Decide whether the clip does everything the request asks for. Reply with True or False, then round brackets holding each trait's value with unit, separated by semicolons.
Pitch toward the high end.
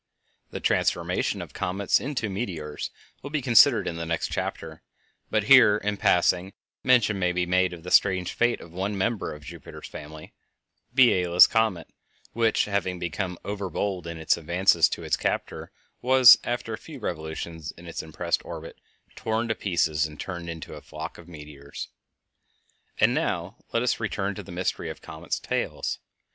False (90 Hz)